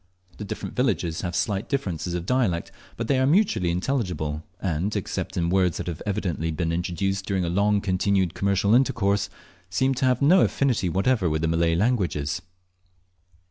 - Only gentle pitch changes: No, average, 4.2 semitones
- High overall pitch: No, very low, 95 Hz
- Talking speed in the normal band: Yes, average, 170 wpm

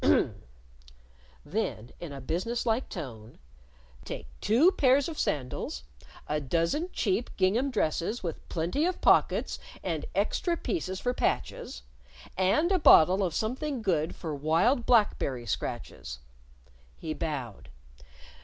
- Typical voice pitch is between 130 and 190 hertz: Yes, medium, 185 Hz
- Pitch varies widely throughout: Yes, wide, 8.6 semitones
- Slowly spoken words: Yes, slow, 130 wpm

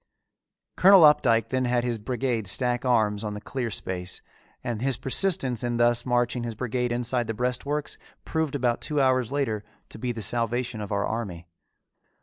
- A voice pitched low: Yes, low, 120 Hz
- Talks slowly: No, average, 170 wpm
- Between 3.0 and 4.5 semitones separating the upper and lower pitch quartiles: No, narrow, 2.5 semitones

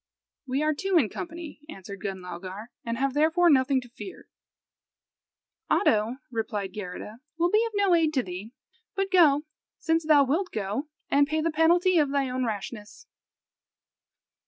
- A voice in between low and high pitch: No, very high, 275 Hz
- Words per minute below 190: Yes, average, 155 wpm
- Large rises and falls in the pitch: Yes, wide, 7.3 semitones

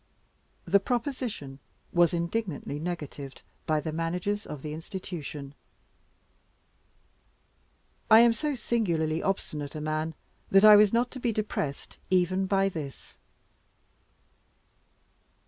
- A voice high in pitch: No, medium, 175 Hz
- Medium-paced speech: No, slow, 110 wpm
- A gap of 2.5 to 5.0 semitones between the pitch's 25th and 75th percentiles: No, wide, 5.4 semitones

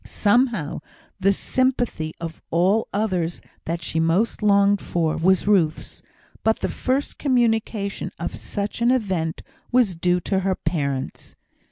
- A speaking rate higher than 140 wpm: No, slow, 135 wpm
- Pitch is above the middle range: Yes, high, 195 Hz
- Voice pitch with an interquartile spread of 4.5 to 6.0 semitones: Yes, average, 5.0 semitones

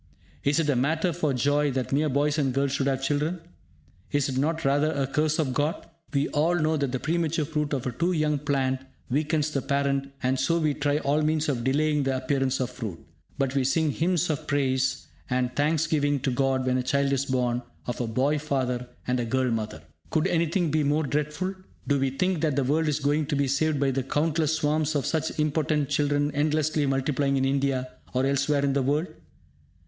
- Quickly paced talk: Yes, fast, 215 wpm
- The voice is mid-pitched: Yes, medium, 145 Hz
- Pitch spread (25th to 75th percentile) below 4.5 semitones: Yes, narrow, 2.4 semitones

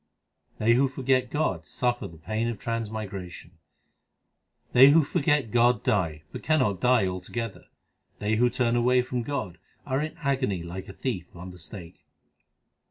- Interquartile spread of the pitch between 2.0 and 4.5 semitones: No, average, 5.1 semitones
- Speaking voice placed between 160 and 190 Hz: No, low, 115 Hz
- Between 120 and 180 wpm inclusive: Yes, average, 160 wpm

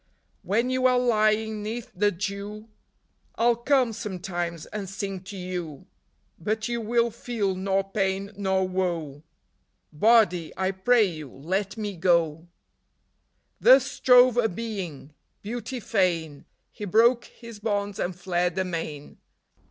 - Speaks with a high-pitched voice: Yes, high, 200 Hz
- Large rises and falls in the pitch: No, average, 4.1 semitones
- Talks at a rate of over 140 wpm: No, slow, 135 wpm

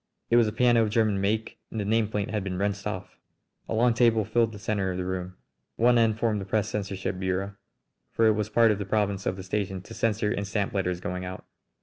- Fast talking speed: Yes, fast, 240 wpm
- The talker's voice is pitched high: No, low, 105 Hz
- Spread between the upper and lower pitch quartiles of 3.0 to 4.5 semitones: No, narrow, 2.5 semitones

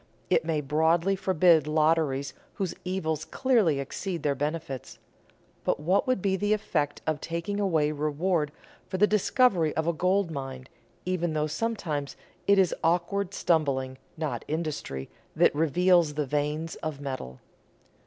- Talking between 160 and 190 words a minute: No, average, 145 wpm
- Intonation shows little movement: No, average, 3.9 semitones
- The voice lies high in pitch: No, medium, 160 Hz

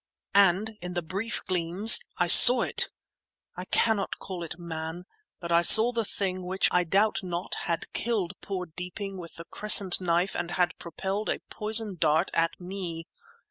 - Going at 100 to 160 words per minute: No, average, 170 wpm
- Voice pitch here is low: No, medium, 180 Hz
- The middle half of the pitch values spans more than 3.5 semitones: No, average, 2.9 semitones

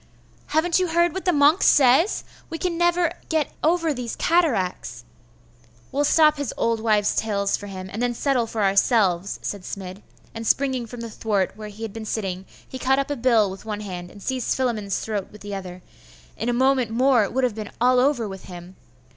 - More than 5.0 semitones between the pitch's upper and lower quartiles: Yes, wide, 5.5 semitones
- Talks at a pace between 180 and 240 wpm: Yes, fast, 205 wpm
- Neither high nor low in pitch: No, high, 230 Hz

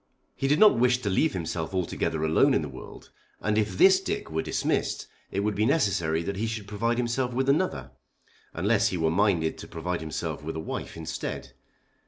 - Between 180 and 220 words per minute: Yes, average, 200 wpm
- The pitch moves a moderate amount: No, wide, 6.5 semitones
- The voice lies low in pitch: Yes, low, 100 Hz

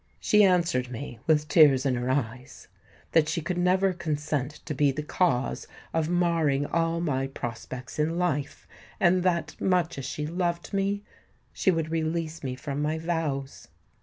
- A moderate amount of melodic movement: Yes, average, 4.0 semitones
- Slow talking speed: No, average, 165 wpm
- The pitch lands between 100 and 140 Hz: No, medium, 155 Hz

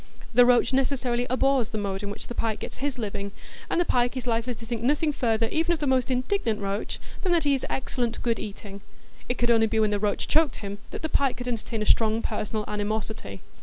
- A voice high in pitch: Yes, high, 235 Hz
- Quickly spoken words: Yes, fast, 235 wpm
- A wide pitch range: No, average, 3.4 semitones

